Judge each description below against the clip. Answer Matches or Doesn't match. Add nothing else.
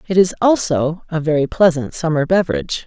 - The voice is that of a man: Doesn't match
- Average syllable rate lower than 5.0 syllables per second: Doesn't match